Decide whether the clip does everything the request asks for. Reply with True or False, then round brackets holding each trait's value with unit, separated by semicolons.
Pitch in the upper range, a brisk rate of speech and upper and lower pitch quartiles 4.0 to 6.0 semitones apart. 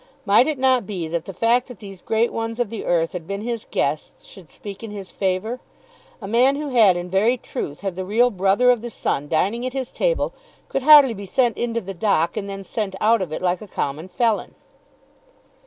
True (210 Hz; 220 wpm; 4.3 semitones)